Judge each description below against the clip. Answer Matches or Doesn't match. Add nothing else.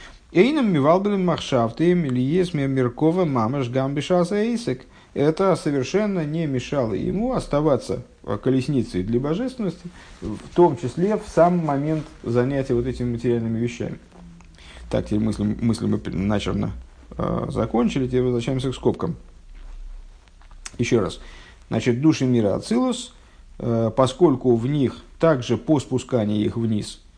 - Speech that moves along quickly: Doesn't match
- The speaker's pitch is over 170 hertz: Doesn't match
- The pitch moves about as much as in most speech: Doesn't match